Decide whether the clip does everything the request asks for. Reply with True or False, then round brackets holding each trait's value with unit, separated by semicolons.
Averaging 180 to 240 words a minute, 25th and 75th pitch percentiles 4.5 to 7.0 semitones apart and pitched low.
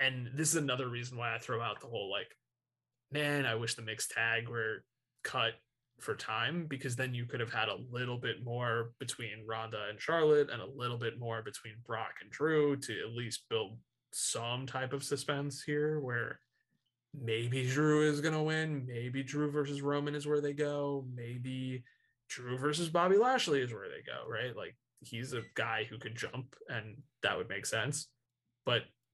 False (190 wpm; 3.5 semitones; 125 Hz)